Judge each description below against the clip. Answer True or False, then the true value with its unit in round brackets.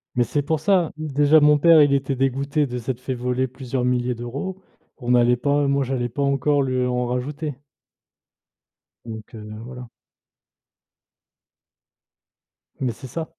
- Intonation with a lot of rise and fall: False (2.8 semitones)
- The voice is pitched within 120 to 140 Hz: True (135 Hz)